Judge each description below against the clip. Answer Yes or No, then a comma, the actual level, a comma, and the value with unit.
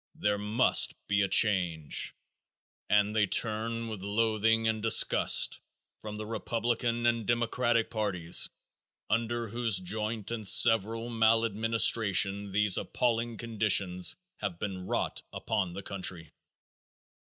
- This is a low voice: Yes, low, 110 Hz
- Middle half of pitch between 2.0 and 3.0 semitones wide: Yes, narrow, 2.4 semitones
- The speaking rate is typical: No, slow, 115 wpm